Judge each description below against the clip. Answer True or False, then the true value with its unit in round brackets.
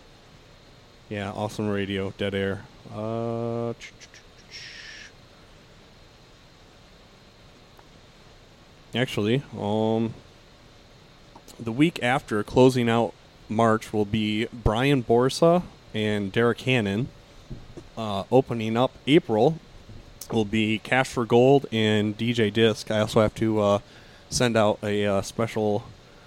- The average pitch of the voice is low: True (115 Hz)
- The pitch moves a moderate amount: False (2.2 semitones)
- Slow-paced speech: True (100 wpm)